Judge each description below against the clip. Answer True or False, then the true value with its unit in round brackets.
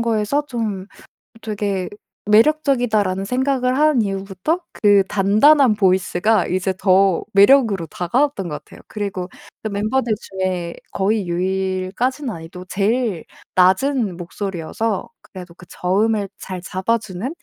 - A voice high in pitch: True (200 Hz)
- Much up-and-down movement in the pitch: False (3.8 semitones)